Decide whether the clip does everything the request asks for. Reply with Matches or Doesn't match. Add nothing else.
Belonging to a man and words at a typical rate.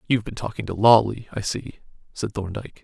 Matches